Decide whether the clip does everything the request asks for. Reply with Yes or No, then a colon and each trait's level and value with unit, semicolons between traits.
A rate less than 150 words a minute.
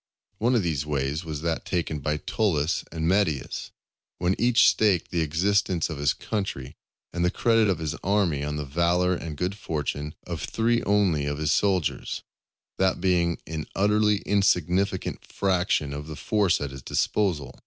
No: average, 165 wpm